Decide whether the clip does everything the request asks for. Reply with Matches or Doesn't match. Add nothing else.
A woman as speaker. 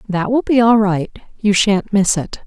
Matches